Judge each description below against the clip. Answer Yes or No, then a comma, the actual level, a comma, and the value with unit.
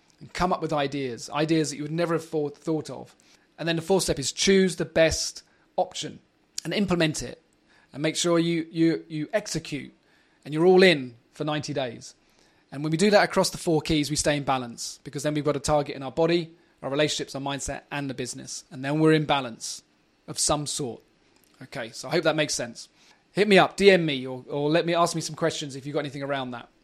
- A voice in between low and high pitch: Yes, medium, 155 Hz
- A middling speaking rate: No, fast, 230 wpm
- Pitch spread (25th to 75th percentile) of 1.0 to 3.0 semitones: Yes, narrow, 2.6 semitones